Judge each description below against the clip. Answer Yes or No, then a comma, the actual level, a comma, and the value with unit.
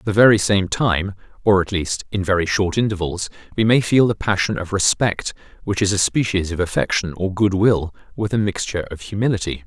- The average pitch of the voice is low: Yes, low, 100 Hz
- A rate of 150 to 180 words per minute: No, fast, 205 wpm